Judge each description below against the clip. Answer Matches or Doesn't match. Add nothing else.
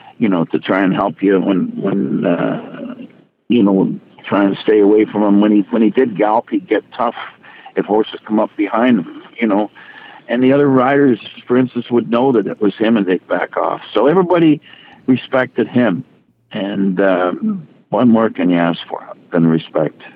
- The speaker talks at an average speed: Matches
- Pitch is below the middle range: Matches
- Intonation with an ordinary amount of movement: Doesn't match